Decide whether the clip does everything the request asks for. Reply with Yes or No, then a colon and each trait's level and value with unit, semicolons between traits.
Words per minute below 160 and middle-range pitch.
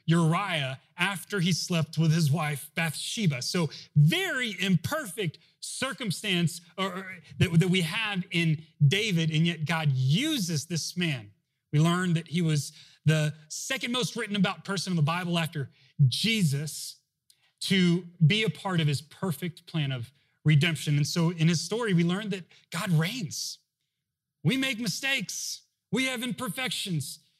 Yes: average, 140 wpm; medium, 165 Hz